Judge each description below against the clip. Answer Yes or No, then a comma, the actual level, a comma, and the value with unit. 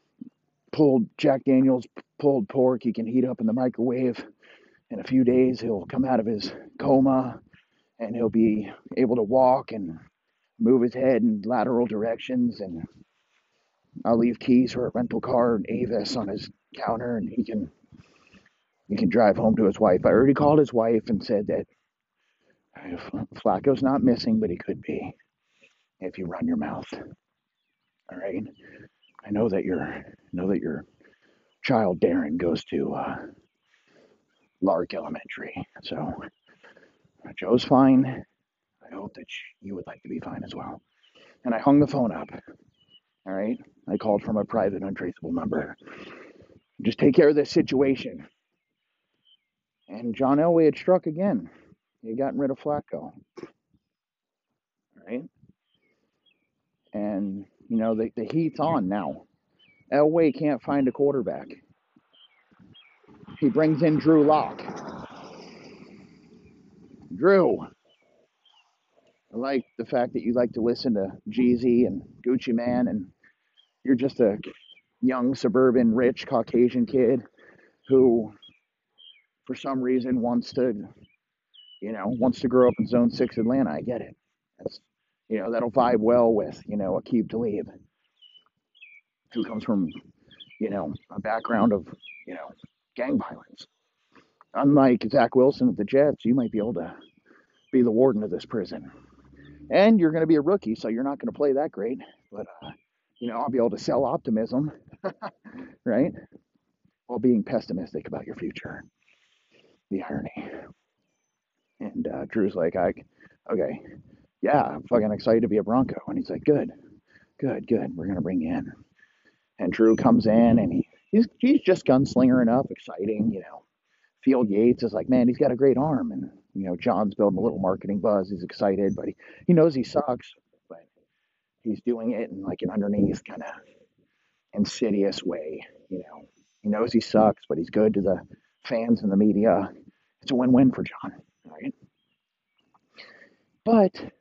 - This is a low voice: Yes, low, 125 Hz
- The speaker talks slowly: No, average, 155 wpm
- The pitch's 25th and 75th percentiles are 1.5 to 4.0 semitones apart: Yes, average, 3.6 semitones